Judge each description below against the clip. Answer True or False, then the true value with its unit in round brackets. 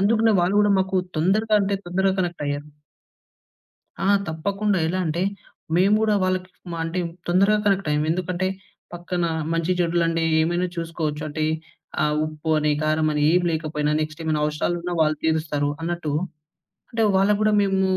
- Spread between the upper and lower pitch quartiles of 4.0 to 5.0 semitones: False (3.5 semitones)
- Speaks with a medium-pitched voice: True (175 Hz)